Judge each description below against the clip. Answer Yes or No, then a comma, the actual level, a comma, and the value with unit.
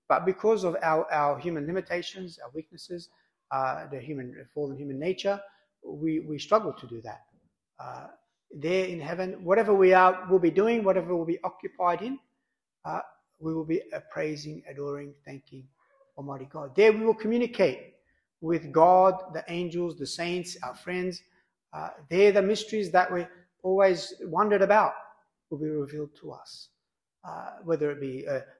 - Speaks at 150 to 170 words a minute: Yes, average, 160 wpm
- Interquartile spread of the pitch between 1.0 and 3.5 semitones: No, average, 4.2 semitones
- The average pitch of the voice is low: No, medium, 175 Hz